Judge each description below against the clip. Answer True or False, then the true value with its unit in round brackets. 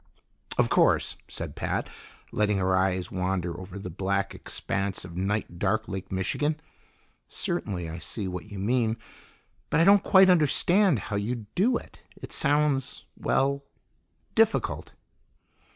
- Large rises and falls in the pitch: True (7.2 semitones)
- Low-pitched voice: True (105 Hz)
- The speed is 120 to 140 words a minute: True (135 wpm)